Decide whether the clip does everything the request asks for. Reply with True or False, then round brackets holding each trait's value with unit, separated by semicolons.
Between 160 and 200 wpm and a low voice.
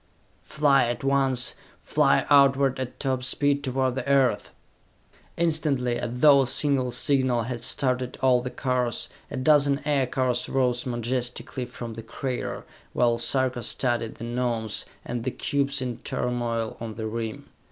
False (145 wpm; 125 Hz)